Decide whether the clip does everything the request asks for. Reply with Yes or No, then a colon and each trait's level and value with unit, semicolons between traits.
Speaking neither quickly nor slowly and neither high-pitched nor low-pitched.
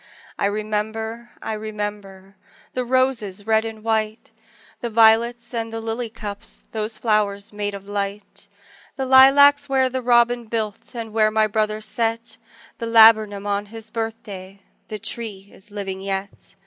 No: average, 150 wpm; high, 220 Hz